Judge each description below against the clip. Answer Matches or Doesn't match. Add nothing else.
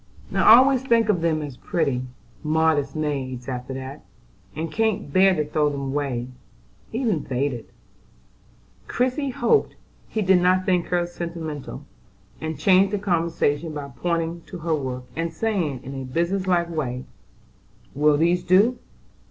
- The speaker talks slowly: Doesn't match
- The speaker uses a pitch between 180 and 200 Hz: Doesn't match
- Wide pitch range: Doesn't match